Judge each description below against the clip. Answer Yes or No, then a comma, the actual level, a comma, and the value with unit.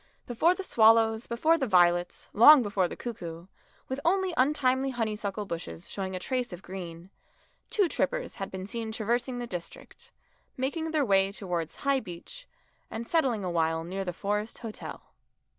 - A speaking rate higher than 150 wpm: Yes, average, 160 wpm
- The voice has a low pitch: No, high, 220 Hz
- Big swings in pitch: Yes, wide, 6.0 semitones